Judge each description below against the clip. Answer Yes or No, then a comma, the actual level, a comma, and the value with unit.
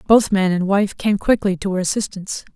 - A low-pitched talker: No, high, 195 Hz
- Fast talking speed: Yes, fast, 210 wpm